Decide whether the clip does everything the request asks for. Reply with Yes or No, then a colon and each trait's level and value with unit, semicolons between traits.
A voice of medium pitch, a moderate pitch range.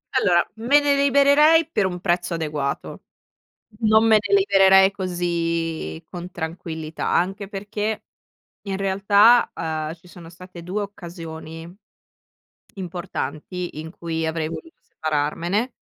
Yes: medium, 180 Hz; average, 3.7 semitones